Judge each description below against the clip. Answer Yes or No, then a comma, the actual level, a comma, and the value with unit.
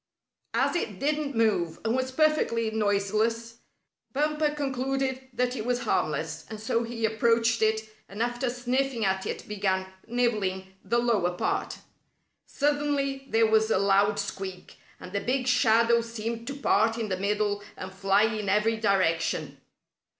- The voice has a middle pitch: No, high, 225 Hz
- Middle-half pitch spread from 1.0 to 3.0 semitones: No, average, 3.7 semitones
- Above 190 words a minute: No, average, 150 wpm